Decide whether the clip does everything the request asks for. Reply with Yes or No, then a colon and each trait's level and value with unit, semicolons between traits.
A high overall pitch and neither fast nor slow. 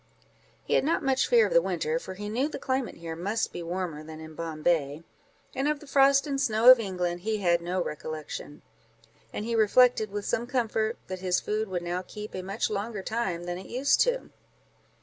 No: high, 210 Hz; fast, 210 wpm